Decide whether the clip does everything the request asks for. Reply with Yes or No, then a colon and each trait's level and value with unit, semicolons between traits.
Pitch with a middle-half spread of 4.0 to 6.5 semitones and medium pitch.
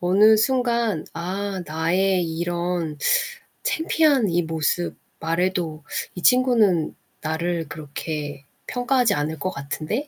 Yes: average, 5.2 semitones; medium, 175 Hz